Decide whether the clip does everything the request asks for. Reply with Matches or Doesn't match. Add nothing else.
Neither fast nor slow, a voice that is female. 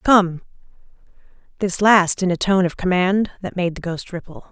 Matches